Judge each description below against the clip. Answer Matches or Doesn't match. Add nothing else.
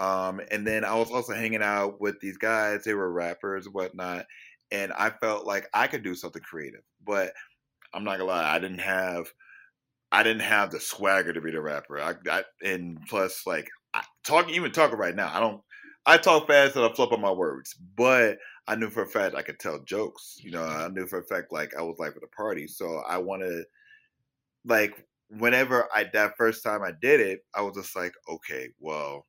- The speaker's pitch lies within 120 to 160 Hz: Doesn't match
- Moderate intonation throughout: Matches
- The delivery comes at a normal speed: Doesn't match